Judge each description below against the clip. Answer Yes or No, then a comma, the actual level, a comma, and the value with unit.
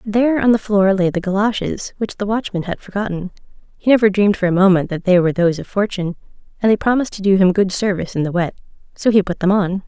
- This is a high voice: Yes, high, 195 Hz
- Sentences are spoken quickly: Yes, fast, 245 wpm